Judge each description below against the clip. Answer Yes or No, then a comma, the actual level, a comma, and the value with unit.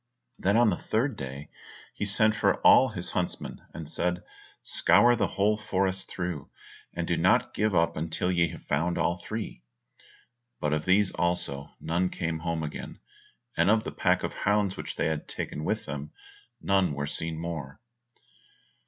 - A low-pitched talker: Yes, very low, 90 Hz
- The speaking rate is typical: Yes, average, 170 wpm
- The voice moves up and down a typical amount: Yes, average, 4.1 semitones